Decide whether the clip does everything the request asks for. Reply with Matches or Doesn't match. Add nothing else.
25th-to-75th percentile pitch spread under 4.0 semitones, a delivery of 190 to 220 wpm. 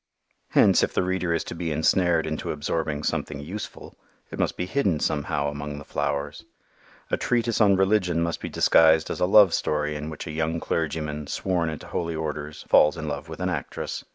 Matches